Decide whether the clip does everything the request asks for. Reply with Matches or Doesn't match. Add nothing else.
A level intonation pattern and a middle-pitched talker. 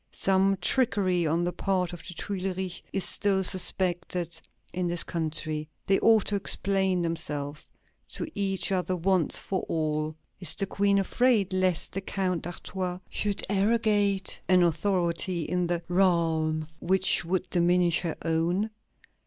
Matches